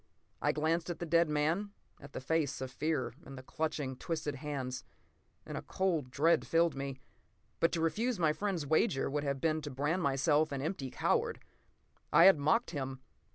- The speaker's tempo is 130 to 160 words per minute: No, average, 185 wpm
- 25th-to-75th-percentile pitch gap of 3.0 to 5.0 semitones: Yes, average, 3.3 semitones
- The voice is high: No, medium, 150 Hz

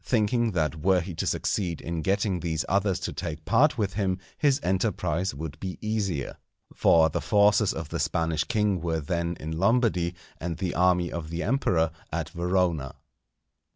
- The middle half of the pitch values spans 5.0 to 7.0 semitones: No, average, 3.7 semitones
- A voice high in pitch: No, very low, 90 Hz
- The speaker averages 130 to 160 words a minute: No, average, 170 wpm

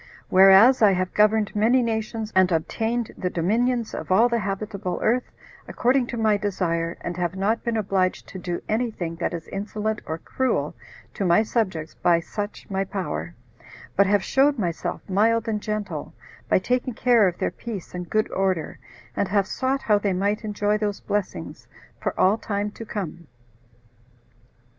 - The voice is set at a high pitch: Yes, high, 205 Hz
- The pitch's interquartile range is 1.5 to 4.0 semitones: Yes, average, 3.3 semitones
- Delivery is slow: No, average, 170 wpm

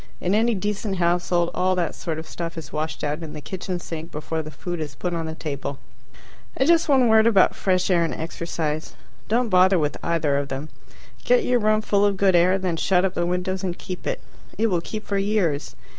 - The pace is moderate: No, fast, 220 wpm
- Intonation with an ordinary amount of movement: Yes, average, 3.7 semitones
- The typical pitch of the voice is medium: Yes, medium, 180 Hz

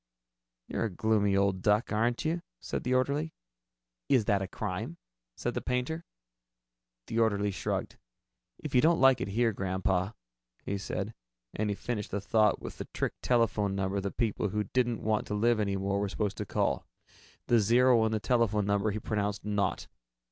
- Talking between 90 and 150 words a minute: No, average, 185 wpm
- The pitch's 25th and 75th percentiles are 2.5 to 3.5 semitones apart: Yes, average, 2.9 semitones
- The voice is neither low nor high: No, low, 105 Hz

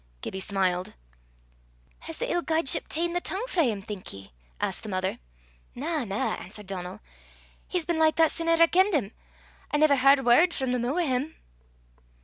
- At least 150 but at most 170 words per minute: No, average, 185 wpm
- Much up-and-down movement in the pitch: Yes, wide, 8.2 semitones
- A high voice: Yes, very high, 280 Hz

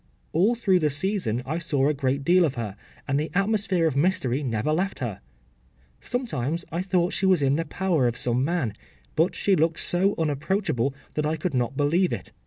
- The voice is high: No, medium, 155 Hz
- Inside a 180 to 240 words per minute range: Yes, fast, 205 wpm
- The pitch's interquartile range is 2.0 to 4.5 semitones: No, average, 5.3 semitones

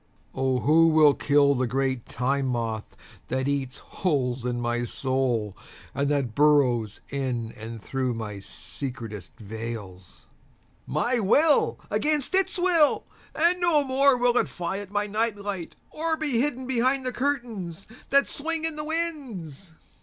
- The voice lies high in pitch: No, medium, 150 Hz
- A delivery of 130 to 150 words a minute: Yes, average, 145 wpm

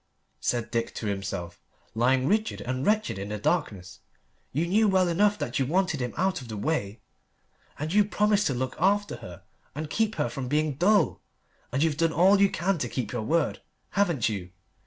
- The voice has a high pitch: No, medium, 150 Hz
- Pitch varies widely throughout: Yes, wide, 8.2 semitones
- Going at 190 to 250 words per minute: Yes, average, 195 wpm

